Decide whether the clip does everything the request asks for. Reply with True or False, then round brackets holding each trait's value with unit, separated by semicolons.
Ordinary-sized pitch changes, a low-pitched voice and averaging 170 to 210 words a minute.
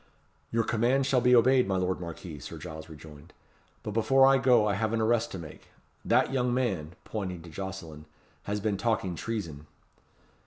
False (5.9 semitones; 105 Hz; 180 wpm)